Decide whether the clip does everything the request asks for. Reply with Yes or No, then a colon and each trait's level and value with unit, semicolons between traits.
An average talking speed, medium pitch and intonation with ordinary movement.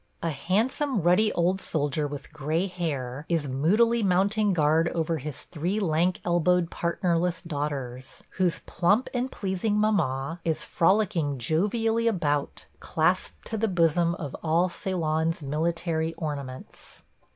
No: slow, 130 wpm; medium, 170 Hz; average, 3.9 semitones